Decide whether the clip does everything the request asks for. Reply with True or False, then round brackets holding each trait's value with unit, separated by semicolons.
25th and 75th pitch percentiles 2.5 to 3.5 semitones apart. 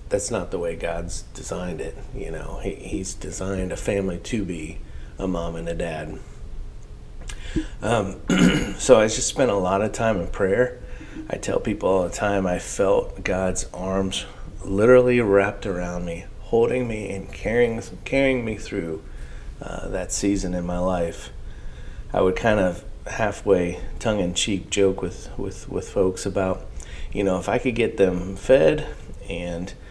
True (3.2 semitones)